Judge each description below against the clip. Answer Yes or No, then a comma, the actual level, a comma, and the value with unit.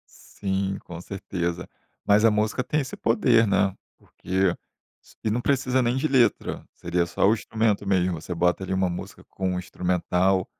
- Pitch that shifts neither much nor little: Yes, average, 4.0 semitones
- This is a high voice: No, very low, 95 Hz